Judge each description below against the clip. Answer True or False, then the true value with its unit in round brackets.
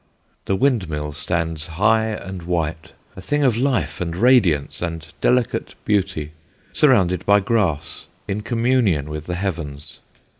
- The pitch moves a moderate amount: False (5.7 semitones)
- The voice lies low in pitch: True (95 Hz)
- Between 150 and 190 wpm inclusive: False (135 wpm)